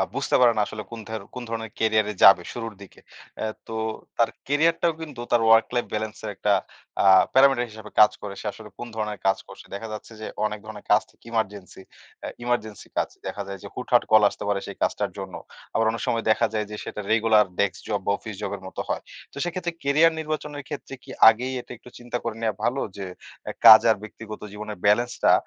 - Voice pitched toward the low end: Yes, low, 110 Hz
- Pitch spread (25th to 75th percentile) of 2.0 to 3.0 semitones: Yes, narrow, 2.4 semitones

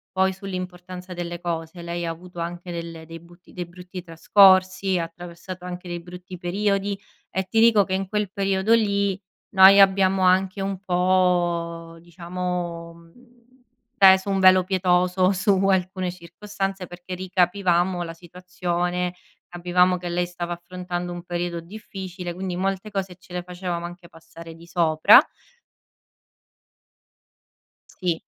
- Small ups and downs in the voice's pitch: Yes, narrow, 1.6 semitones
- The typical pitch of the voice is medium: Yes, medium, 180 Hz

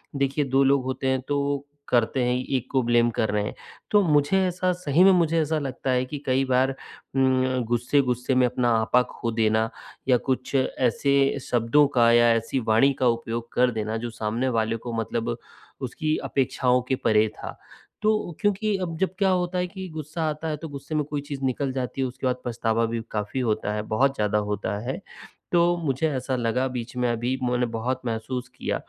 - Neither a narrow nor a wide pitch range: Yes, average, 3.5 semitones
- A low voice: Yes, low, 130 Hz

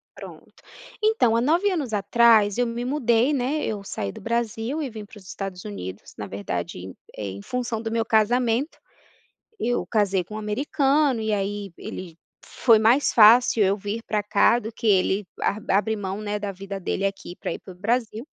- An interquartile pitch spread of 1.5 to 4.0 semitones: Yes, average, 3.4 semitones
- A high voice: Yes, high, 220 Hz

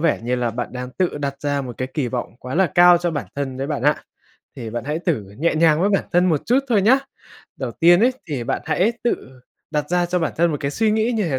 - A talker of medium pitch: Yes, medium, 155 Hz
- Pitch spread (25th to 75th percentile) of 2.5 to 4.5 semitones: No, average, 5.1 semitones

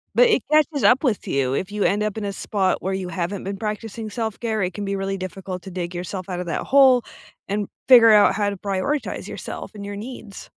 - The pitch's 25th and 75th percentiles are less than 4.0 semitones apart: Yes, average, 2.9 semitones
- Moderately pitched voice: No, high, 200 Hz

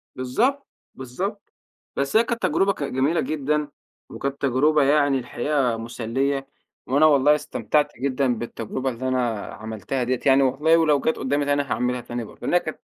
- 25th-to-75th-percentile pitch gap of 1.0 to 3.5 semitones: Yes, average, 3.1 semitones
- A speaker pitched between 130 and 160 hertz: Yes, low, 135 Hz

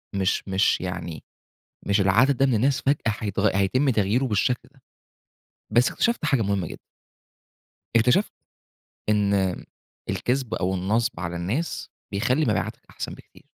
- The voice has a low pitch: Yes, low, 110 Hz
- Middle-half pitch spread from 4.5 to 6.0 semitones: Yes, average, 5.0 semitones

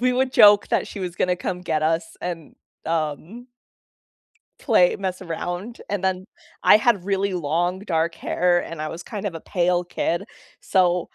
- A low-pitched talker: No, medium, 180 Hz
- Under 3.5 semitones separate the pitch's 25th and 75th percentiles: Yes, average, 3.0 semitones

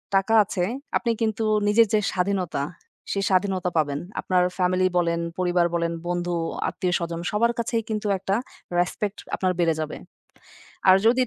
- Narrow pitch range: No, average, 3.0 semitones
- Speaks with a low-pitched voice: No, medium, 185 Hz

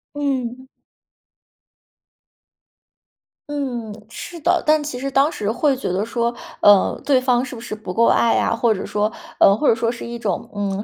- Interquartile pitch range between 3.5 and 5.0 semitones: Yes, average, 4.1 semitones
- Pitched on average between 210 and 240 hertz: Yes, high, 235 Hz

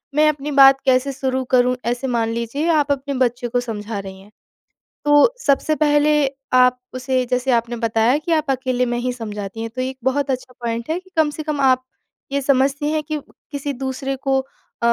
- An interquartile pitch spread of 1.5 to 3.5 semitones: Yes, average, 2.9 semitones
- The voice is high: Yes, very high, 260 Hz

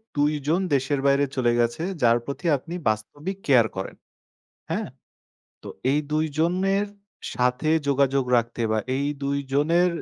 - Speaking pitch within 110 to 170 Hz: Yes, medium, 140 Hz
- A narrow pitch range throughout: No, average, 4.2 semitones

